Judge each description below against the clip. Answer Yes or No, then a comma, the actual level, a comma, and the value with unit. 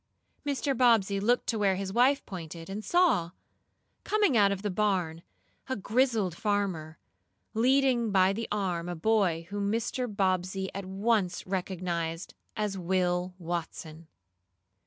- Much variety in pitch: No, average, 4.0 semitones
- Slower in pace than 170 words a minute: Yes, slow, 135 wpm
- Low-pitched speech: No, high, 195 Hz